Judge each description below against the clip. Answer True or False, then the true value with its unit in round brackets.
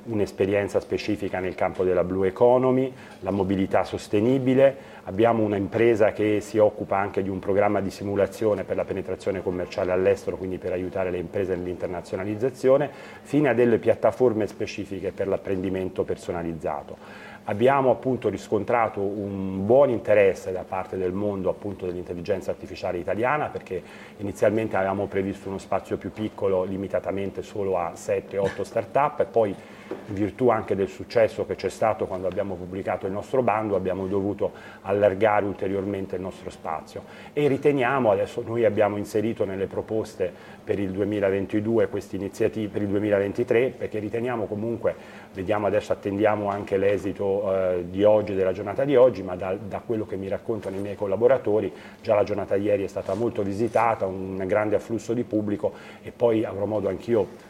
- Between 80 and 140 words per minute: False (155 wpm)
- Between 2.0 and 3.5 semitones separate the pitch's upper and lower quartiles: True (2.9 semitones)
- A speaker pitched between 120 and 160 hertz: False (100 Hz)